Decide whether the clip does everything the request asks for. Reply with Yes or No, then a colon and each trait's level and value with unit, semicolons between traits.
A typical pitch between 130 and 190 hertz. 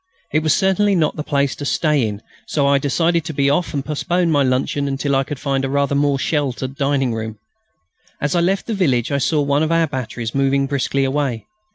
Yes: medium, 140 Hz